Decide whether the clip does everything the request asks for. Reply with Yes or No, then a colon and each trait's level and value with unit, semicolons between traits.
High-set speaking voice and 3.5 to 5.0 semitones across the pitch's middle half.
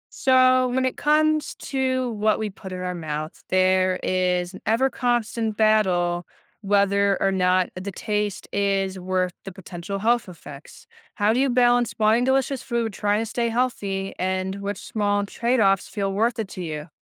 Yes: high, 205 Hz; average, 4.2 semitones